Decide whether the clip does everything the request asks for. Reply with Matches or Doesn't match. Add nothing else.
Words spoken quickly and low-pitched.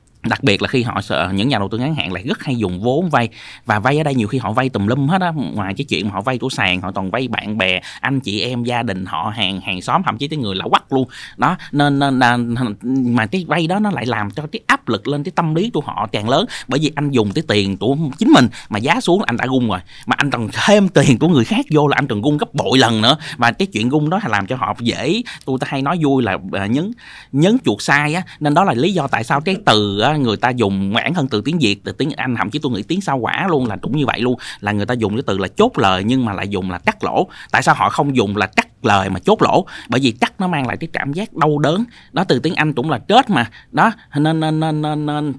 Matches